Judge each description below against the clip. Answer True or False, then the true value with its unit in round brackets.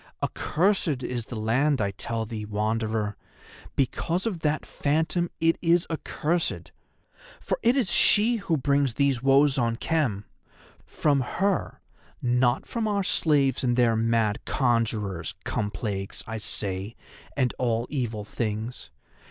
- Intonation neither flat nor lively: False (6.0 semitones)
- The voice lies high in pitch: False (125 Hz)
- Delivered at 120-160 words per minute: True (135 wpm)